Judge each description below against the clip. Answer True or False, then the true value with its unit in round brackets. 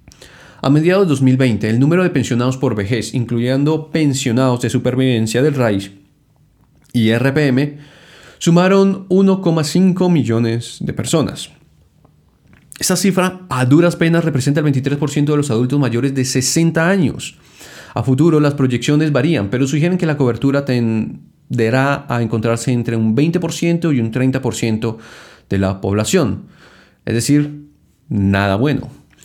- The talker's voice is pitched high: False (135 Hz)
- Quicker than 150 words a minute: False (130 wpm)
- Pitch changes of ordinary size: True (4.7 semitones)